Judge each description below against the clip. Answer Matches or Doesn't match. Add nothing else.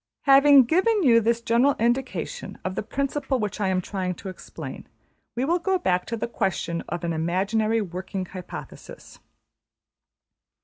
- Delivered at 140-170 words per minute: Matches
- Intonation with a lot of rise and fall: Matches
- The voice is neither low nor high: Doesn't match